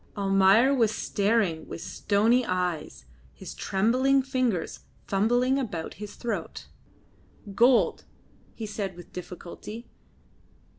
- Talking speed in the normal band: No, slow, 100 wpm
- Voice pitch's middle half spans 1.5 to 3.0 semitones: No, average, 4.9 semitones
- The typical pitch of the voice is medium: No, high, 205 Hz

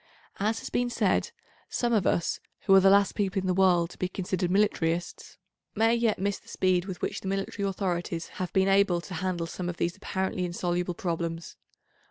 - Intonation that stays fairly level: Yes, narrow, 2.1 semitones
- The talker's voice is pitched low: No, medium, 185 Hz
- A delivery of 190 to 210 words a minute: Yes, average, 200 wpm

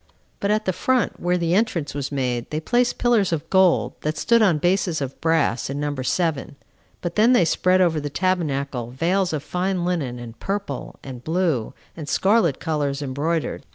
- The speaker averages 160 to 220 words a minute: Yes, average, 185 wpm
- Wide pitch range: No, average, 4.7 semitones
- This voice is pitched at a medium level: Yes, medium, 165 Hz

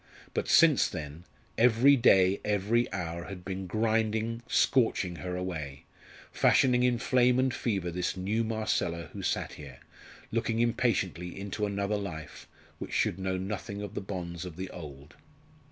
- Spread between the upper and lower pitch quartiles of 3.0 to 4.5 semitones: Yes, average, 4.2 semitones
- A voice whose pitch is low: Yes, low, 100 Hz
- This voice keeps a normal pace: Yes, average, 150 wpm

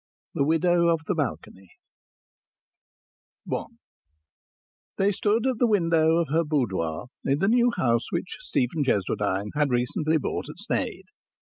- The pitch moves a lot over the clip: Yes, wide, 6.2 semitones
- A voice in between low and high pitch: Yes, medium, 155 Hz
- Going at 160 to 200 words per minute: No, slow, 135 wpm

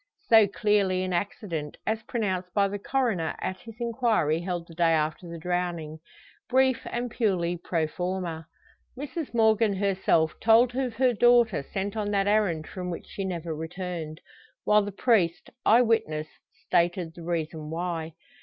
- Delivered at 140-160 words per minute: Yes, average, 155 wpm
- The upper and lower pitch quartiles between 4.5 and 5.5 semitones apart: Yes, average, 4.8 semitones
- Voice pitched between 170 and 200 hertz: Yes, medium, 185 Hz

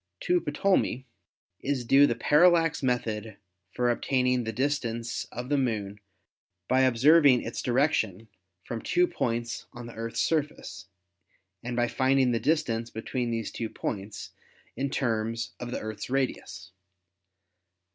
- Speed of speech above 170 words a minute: No, slow, 135 wpm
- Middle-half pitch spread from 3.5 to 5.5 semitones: No, average, 3.1 semitones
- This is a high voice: No, low, 120 Hz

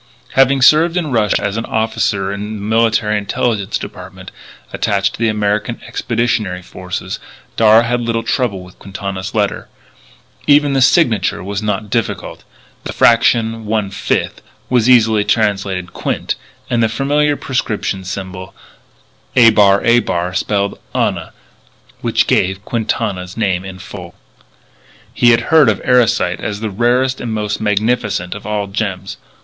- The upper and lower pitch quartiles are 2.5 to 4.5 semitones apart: Yes, average, 3.1 semitones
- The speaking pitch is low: Yes, low, 110 Hz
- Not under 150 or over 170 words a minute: No, slow, 135 wpm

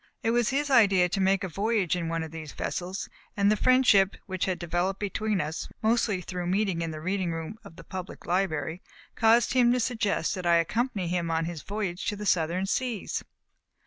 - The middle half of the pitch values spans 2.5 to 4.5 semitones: Yes, average, 4.0 semitones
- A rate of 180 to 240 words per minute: Yes, fast, 205 wpm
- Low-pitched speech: No, high, 190 Hz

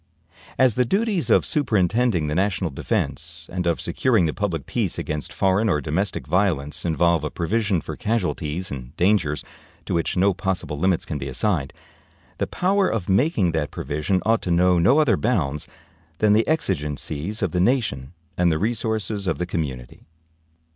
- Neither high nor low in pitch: No, very low, 90 Hz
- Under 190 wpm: Yes, average, 170 wpm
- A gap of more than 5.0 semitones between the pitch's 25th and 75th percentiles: Yes, wide, 5.6 semitones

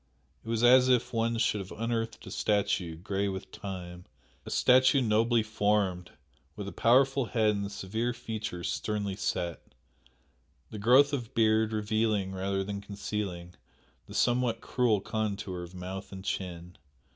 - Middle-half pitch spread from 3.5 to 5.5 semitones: No, average, 3.1 semitones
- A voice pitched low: Yes, low, 105 Hz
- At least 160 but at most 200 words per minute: No, average, 145 wpm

